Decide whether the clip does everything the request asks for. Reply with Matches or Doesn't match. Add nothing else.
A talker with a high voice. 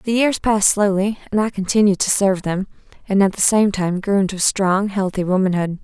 Matches